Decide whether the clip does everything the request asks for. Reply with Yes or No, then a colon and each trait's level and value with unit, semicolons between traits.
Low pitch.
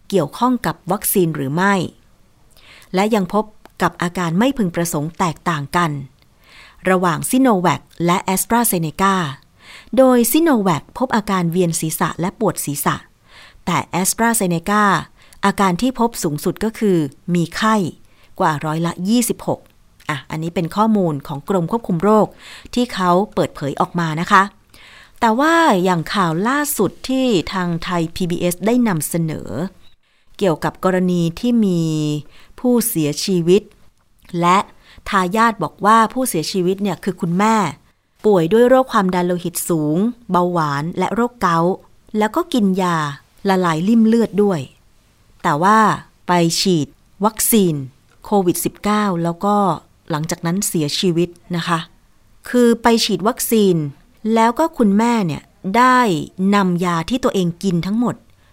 No: medium, 185 Hz